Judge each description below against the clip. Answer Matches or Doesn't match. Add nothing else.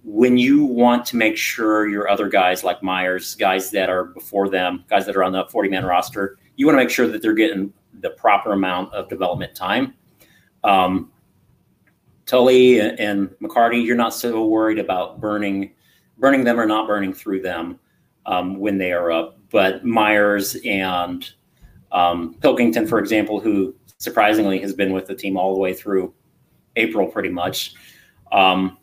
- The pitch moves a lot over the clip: Doesn't match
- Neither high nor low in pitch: Doesn't match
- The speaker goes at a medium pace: Matches